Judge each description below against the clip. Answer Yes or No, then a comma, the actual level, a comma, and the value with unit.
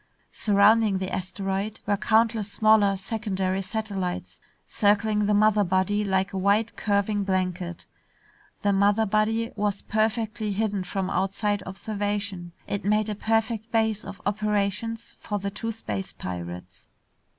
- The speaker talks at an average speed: No, slow, 130 wpm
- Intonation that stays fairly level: Yes, narrow, 2.1 semitones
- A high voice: Yes, high, 205 Hz